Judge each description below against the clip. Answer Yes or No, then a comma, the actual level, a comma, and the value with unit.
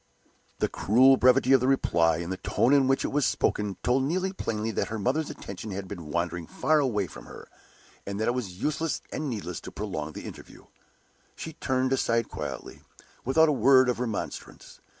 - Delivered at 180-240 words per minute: Yes, average, 190 wpm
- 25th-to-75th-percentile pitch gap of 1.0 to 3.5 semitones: No, wide, 5.5 semitones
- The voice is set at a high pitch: No, low, 120 Hz